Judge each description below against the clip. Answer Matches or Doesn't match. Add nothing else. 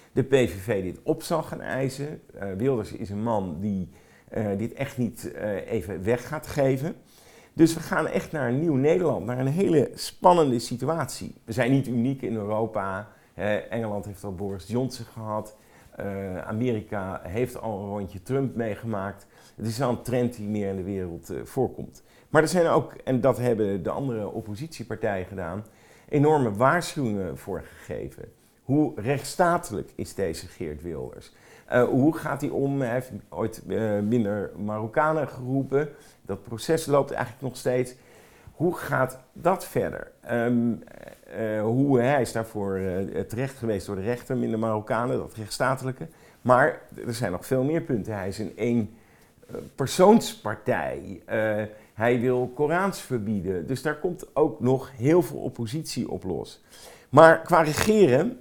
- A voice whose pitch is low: Matches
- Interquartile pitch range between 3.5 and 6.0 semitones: Matches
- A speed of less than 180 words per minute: Matches